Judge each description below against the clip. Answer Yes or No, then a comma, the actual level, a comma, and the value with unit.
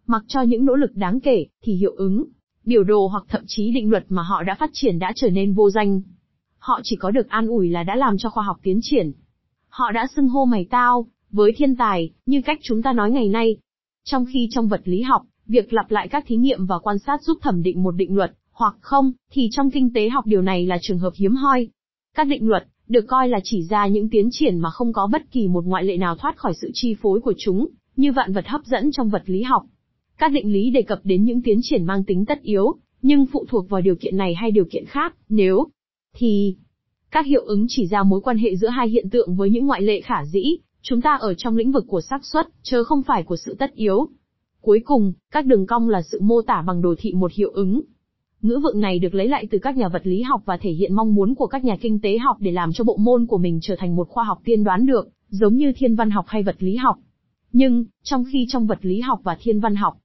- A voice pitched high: Yes, high, 220 Hz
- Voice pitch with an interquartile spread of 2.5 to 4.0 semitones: No, average, 4.4 semitones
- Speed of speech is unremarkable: No, fast, 260 wpm